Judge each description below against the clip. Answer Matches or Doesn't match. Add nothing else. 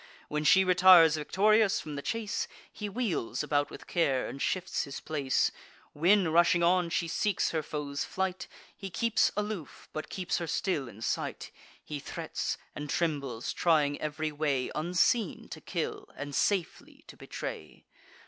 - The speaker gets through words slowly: Doesn't match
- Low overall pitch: Doesn't match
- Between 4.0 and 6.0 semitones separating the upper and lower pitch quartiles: Matches